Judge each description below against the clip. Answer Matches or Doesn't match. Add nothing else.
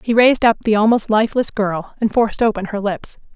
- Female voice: Matches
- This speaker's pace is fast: Matches